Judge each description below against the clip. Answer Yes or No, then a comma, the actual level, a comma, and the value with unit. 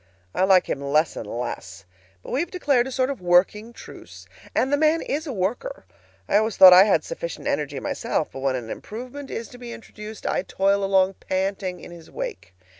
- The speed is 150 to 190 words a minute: No, fast, 205 wpm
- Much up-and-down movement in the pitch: Yes, wide, 6.4 semitones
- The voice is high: Yes, high, 210 Hz